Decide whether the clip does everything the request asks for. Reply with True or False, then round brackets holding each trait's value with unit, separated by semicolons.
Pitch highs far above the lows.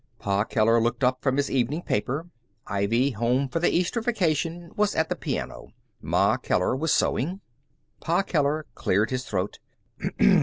True (6.1 semitones)